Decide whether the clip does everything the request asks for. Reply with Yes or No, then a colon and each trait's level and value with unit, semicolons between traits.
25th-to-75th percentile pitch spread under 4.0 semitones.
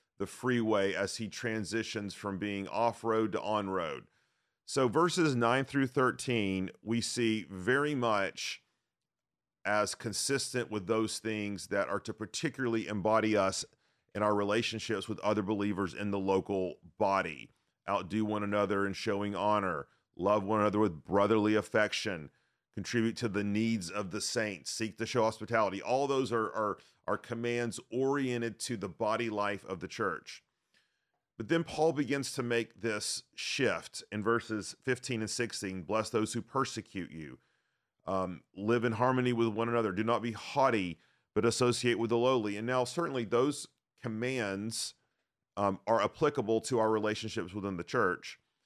Yes: narrow, 2.6 semitones